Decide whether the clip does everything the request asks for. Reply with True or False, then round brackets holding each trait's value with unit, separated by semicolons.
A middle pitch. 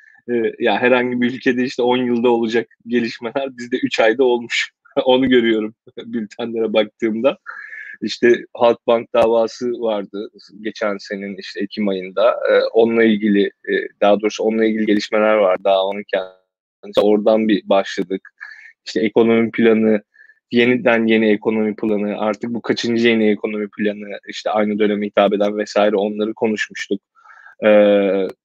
False (110 Hz)